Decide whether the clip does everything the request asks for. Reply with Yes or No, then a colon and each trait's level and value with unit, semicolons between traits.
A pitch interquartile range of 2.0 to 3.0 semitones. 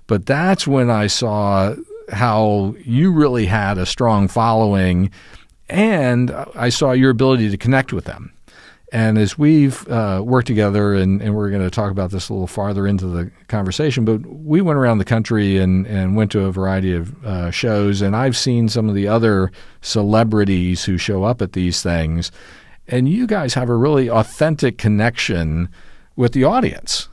No: average, 4.5 semitones